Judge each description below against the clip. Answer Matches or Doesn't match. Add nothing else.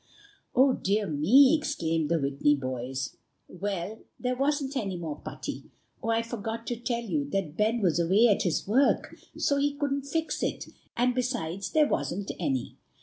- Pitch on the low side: Doesn't match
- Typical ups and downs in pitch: Doesn't match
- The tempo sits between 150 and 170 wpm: Matches